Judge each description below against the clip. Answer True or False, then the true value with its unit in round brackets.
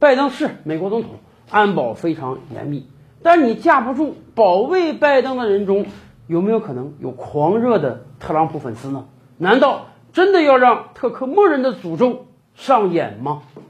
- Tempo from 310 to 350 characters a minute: False (245 characters per minute)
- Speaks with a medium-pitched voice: False (200 Hz)